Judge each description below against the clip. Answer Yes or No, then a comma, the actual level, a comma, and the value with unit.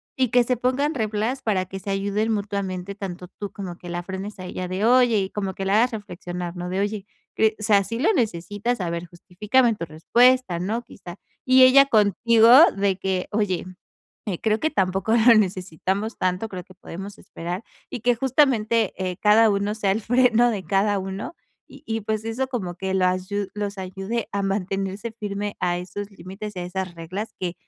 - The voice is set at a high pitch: Yes, high, 200 Hz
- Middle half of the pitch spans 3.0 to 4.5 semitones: Yes, average, 3.3 semitones